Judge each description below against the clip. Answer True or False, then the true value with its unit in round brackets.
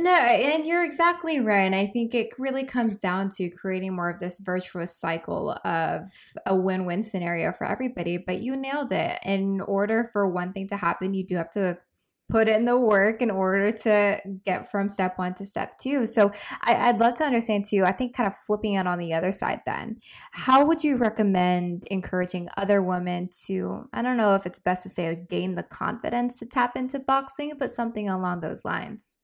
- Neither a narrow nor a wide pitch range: True (4.7 semitones)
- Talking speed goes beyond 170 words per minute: True (205 wpm)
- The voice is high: True (200 Hz)